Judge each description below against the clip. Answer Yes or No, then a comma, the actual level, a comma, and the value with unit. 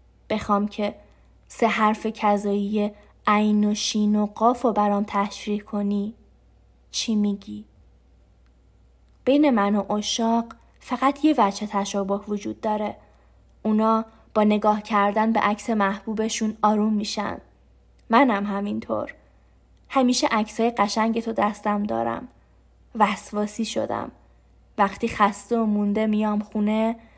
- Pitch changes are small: Yes, narrow, 1.5 semitones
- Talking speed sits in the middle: Yes, average, 115 wpm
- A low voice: No, high, 210 Hz